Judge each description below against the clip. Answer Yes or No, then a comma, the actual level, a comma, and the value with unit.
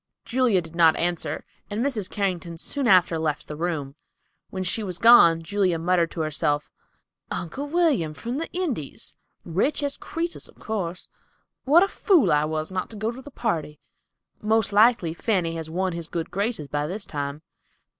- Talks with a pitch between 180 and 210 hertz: Yes, medium, 185 Hz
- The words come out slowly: No, average, 175 wpm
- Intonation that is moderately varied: No, wide, 6.1 semitones